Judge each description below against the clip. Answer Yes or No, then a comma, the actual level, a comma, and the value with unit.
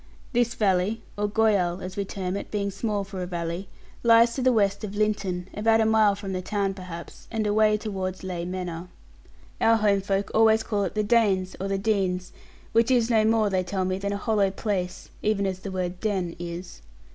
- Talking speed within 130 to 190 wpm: No, fast, 205 wpm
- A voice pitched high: Yes, high, 200 Hz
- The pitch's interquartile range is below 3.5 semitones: Yes, narrow, 2.6 semitones